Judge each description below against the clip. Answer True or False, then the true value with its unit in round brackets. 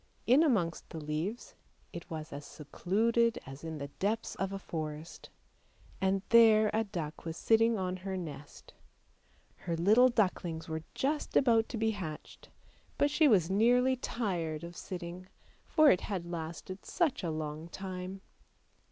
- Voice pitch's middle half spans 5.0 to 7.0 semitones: True (5.6 semitones)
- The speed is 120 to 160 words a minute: True (150 wpm)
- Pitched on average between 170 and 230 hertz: True (185 Hz)